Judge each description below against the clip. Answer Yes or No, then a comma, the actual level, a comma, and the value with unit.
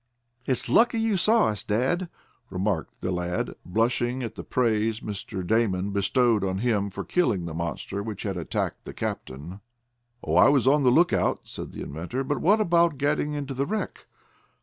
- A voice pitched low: Yes, low, 115 Hz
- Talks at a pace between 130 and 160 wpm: No, average, 175 wpm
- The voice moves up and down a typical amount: No, wide, 7.1 semitones